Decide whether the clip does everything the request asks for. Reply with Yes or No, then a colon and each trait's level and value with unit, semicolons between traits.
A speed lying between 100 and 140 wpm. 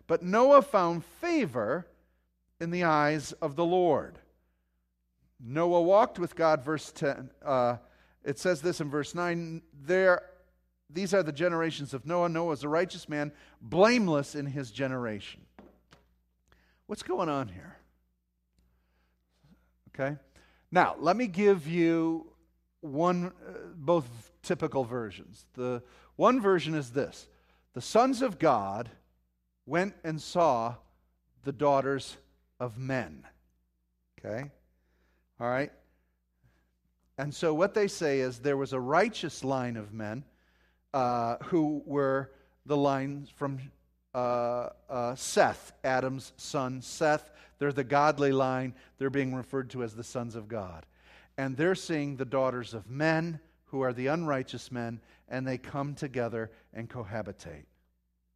Yes: slow, 135 wpm